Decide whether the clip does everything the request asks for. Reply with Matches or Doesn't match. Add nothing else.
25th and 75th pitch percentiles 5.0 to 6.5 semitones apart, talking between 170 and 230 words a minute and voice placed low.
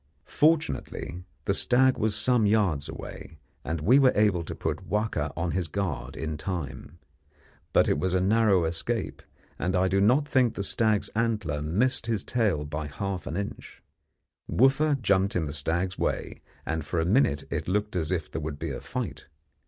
Matches